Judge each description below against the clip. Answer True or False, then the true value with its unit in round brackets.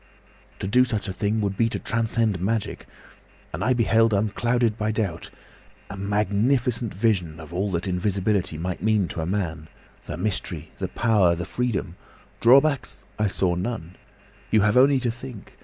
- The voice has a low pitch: True (105 Hz)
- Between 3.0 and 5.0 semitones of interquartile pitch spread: True (3.8 semitones)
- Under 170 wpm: True (160 wpm)